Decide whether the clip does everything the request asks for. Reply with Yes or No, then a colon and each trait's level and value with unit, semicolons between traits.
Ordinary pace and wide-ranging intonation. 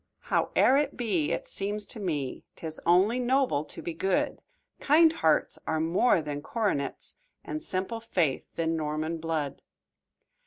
Yes: average, 145 wpm; wide, 6.4 semitones